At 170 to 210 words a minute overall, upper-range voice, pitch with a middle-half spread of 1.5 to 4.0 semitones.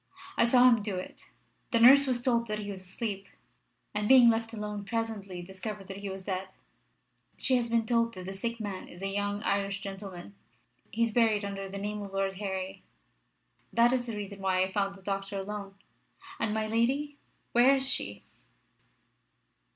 Yes: average, 180 wpm; high, 205 Hz; average, 3.0 semitones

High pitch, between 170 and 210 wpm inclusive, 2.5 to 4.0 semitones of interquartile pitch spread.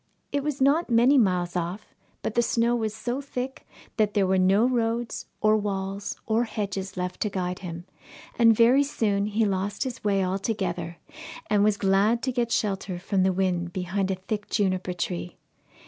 Yes: high, 205 Hz; average, 180 wpm; average, 3.6 semitones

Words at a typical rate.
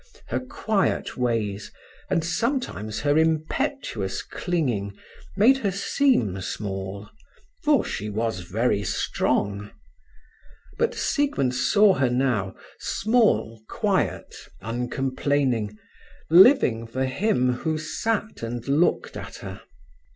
No: slow, 100 wpm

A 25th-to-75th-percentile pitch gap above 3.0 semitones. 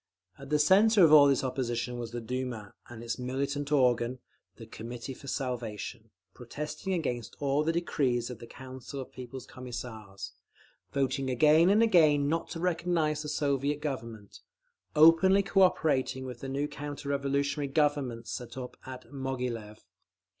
Yes: average, 3.5 semitones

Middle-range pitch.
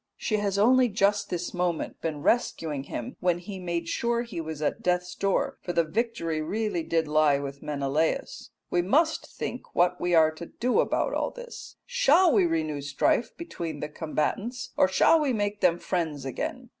Yes: medium, 180 Hz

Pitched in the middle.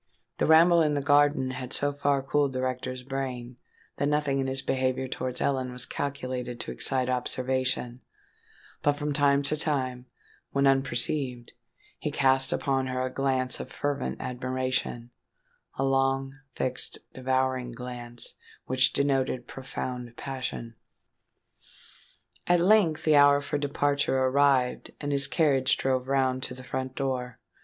No: low, 130 Hz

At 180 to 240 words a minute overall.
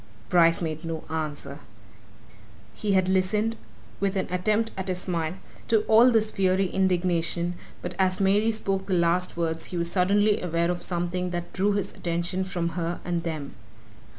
No: average, 165 wpm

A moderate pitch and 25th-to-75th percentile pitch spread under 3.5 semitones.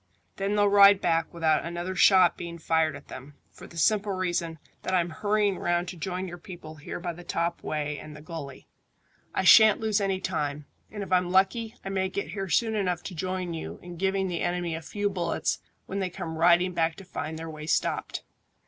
Yes: medium, 175 Hz; average, 2.9 semitones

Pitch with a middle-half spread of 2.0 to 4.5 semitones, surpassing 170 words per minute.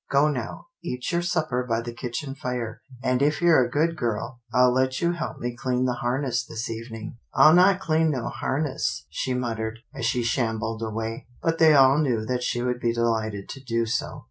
Yes: average, 3.3 semitones; fast, 205 wpm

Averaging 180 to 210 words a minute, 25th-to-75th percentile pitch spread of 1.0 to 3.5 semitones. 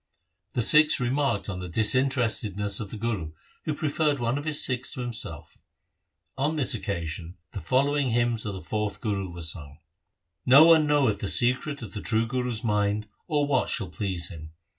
No: average, 185 wpm; wide, 5.6 semitones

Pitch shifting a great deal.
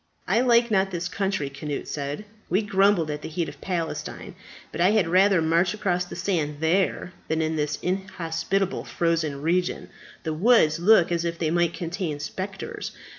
No: average, 3.3 semitones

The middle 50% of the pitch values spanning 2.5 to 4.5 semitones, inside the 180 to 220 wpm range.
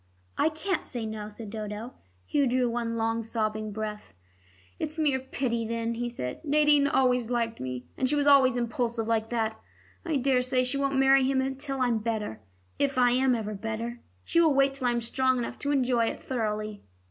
Yes: average, 3.2 semitones; average, 195 wpm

